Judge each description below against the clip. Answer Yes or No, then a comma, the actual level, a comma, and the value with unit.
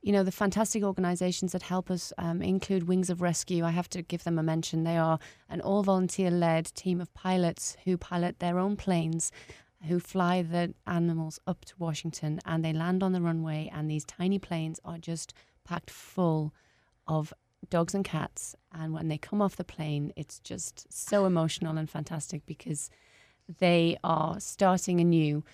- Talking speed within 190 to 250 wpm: No, average, 180 wpm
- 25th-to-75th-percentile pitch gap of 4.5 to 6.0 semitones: No, narrow, 2.4 semitones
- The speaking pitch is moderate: Yes, medium, 170 Hz